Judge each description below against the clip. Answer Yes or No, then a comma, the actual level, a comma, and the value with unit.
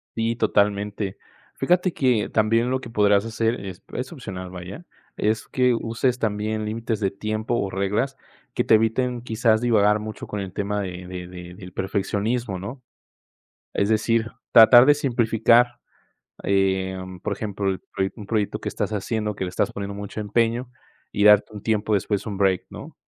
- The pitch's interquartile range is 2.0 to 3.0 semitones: Yes, average, 2.7 semitones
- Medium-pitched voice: No, low, 105 Hz